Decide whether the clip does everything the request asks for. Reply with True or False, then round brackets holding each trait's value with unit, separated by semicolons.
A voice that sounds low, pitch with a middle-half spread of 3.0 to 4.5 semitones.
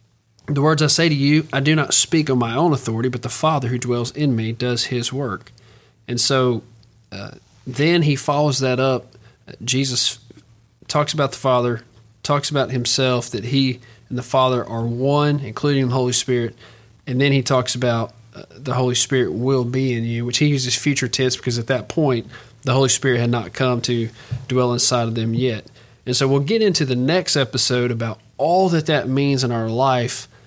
False (125 Hz; 2.6 semitones)